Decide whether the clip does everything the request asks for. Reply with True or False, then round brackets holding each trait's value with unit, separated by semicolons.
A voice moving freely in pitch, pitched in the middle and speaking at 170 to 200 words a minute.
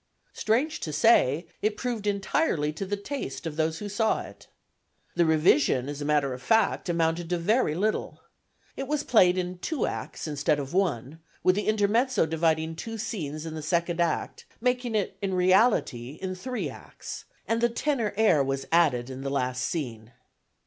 True (6.3 semitones; 175 Hz; 175 wpm)